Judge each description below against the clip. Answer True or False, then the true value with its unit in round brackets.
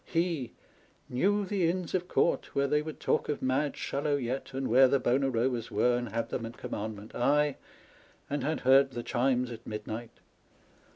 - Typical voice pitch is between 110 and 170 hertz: True (135 Hz)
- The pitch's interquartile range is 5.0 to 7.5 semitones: False (3.6 semitones)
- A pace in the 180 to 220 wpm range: True (185 wpm)